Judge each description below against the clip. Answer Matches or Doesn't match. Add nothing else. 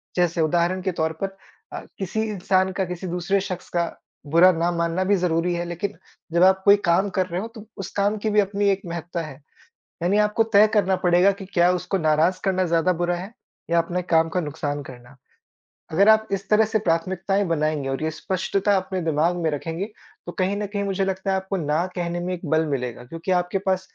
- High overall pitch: Doesn't match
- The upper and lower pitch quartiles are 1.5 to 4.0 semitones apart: Matches